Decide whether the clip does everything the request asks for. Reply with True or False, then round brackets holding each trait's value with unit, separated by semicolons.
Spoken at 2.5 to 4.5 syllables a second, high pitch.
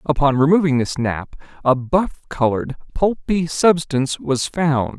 False (4.3 syllables/s; 145 Hz)